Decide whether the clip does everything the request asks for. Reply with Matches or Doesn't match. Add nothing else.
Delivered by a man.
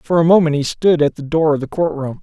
Matches